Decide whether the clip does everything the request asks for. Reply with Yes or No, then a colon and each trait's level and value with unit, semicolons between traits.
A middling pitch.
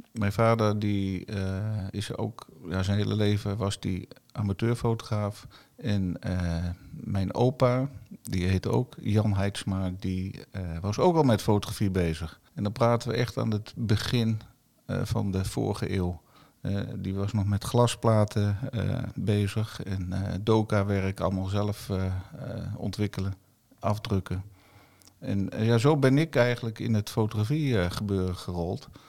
No: low, 105 Hz